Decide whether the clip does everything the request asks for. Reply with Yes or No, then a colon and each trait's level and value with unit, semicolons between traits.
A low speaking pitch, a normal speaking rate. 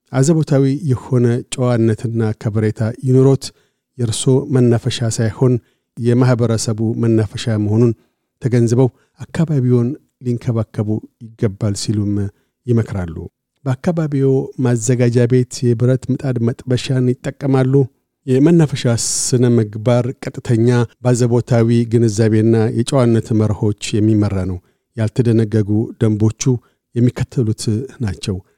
Yes: low, 120 Hz; average, 80 wpm